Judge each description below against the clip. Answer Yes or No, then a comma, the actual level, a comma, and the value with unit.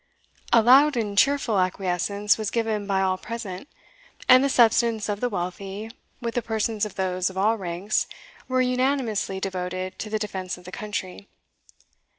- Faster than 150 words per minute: Yes, average, 160 wpm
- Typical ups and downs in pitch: Yes, average, 3.6 semitones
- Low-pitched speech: No, high, 210 Hz